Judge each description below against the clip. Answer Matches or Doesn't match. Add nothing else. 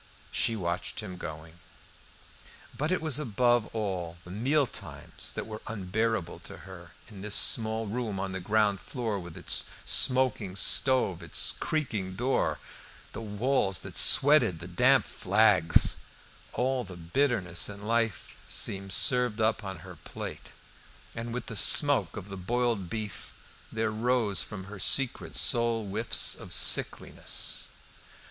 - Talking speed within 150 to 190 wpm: Doesn't match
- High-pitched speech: Doesn't match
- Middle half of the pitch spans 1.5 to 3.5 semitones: Doesn't match